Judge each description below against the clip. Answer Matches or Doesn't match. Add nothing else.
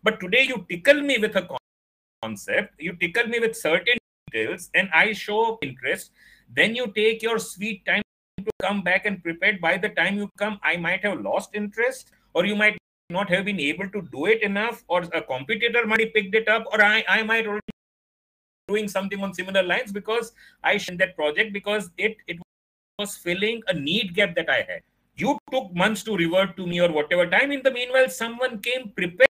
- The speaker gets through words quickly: Matches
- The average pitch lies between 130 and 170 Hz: Doesn't match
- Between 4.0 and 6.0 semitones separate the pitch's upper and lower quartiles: Doesn't match